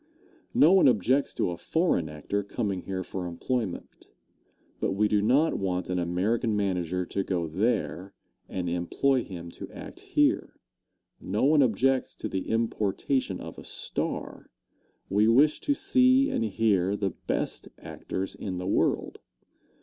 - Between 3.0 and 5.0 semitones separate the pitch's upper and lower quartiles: No, wide, 5.4 semitones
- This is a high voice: No, low, 100 Hz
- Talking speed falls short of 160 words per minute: Yes, average, 150 wpm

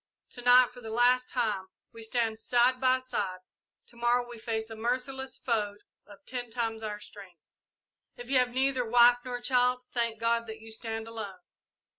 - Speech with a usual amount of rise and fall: No, narrow, 2.1 semitones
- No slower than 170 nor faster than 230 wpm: Yes, average, 180 wpm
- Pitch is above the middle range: Yes, high, 240 Hz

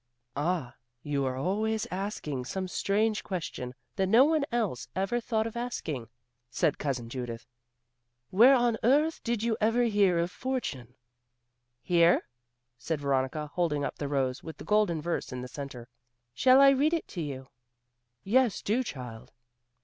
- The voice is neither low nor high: Yes, medium, 180 Hz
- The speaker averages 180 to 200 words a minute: No, average, 155 wpm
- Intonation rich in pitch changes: Yes, wide, 8.8 semitones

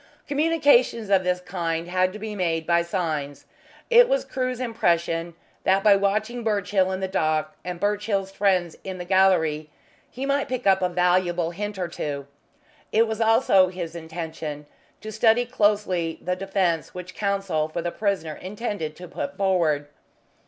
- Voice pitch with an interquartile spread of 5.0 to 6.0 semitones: No, average, 3.6 semitones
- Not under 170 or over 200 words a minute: No, average, 160 wpm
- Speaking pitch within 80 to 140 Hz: No, medium, 185 Hz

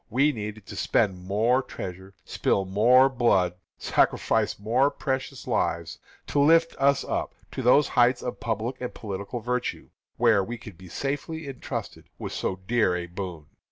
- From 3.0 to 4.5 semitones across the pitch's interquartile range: No, wide, 5.4 semitones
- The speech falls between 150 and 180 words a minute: Yes, average, 160 wpm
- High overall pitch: No, low, 115 Hz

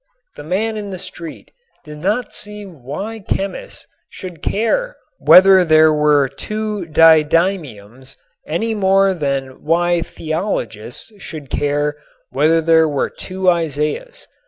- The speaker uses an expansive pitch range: No, average, 4.7 semitones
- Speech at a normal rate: No, slow, 120 wpm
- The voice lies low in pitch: No, medium, 165 Hz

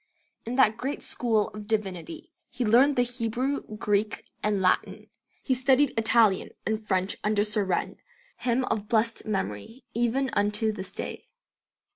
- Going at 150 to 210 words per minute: No, average, 140 wpm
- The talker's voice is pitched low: No, high, 220 Hz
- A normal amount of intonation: Yes, average, 3.2 semitones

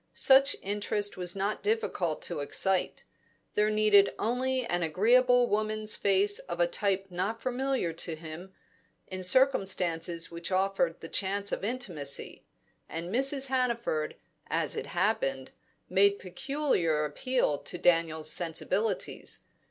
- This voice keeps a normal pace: No, slow, 125 wpm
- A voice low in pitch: No, high, 195 Hz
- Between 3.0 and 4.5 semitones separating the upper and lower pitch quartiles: No, wide, 5.4 semitones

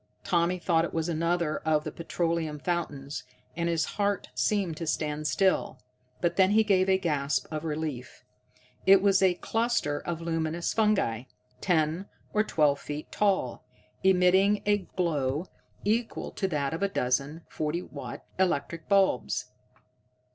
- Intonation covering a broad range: No, average, 3.8 semitones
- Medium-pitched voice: Yes, medium, 170 Hz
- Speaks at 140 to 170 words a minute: Yes, average, 145 wpm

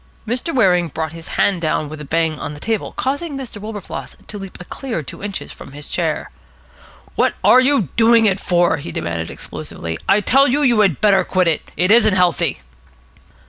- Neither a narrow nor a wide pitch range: No, wide, 5.9 semitones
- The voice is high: Yes, high, 195 Hz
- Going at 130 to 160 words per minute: No, average, 195 wpm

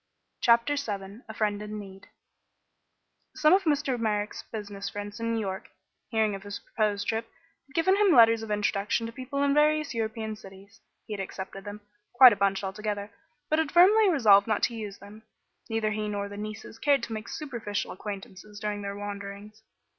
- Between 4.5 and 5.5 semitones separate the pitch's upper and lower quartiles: No, average, 2.7 semitones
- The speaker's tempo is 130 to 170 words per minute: No, average, 185 wpm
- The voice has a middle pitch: No, high, 215 Hz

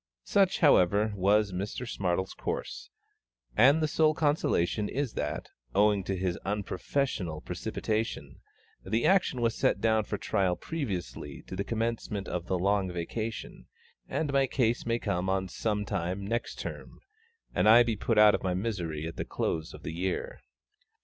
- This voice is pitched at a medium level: No, low, 105 Hz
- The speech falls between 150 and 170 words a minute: Yes, average, 160 wpm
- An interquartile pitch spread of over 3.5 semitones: Yes, average, 4.0 semitones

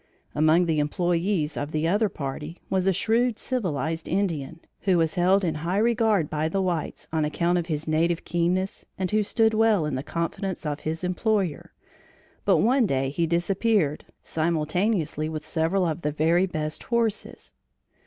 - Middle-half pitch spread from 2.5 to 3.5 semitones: No, average, 4.0 semitones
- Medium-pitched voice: Yes, medium, 170 Hz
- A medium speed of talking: Yes, average, 165 wpm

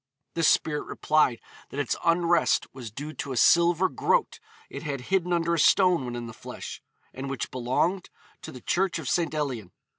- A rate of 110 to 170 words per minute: No, average, 185 wpm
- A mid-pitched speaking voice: Yes, medium, 155 Hz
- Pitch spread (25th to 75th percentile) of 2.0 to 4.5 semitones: No, average, 4.9 semitones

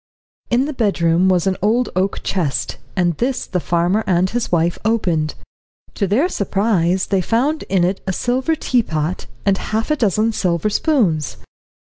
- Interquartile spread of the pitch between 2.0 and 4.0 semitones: No, average, 4.9 semitones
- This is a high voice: Yes, high, 195 Hz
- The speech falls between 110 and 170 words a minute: Yes, average, 160 wpm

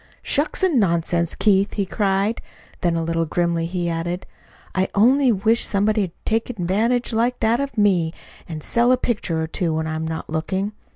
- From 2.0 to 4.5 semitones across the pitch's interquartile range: No, average, 5.2 semitones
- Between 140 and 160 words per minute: No, average, 175 wpm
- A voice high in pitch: Yes, high, 195 Hz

